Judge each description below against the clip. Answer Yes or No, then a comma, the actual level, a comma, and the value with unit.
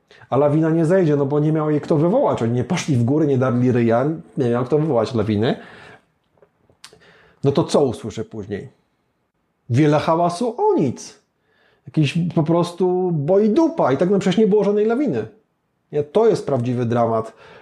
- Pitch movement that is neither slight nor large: No, wide, 5.8 semitones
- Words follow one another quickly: Yes, fast, 175 wpm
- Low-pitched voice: No, medium, 150 Hz